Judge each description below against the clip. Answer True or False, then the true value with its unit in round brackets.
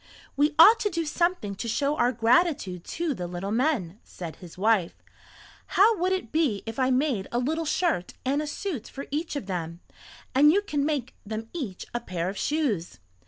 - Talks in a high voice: True (260 Hz)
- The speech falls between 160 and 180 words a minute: False (195 wpm)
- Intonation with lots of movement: True (7.9 semitones)